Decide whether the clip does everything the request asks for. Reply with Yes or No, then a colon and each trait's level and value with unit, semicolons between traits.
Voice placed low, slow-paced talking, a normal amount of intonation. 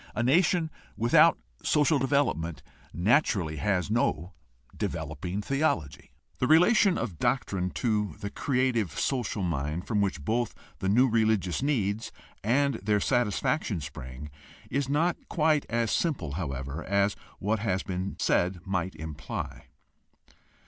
No: low, 105 Hz; slow, 130 wpm; wide, 6.9 semitones